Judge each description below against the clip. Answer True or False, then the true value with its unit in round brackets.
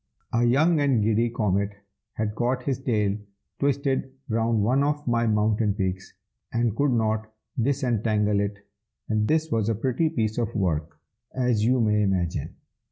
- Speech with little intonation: False (3.4 semitones)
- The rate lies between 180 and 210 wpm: False (155 wpm)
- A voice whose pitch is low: True (115 Hz)